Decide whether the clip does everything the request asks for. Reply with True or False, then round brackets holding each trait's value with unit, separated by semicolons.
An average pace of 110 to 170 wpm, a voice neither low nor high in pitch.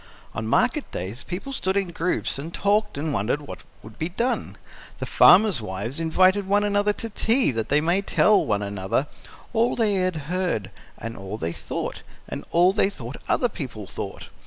False (185 wpm; 170 Hz)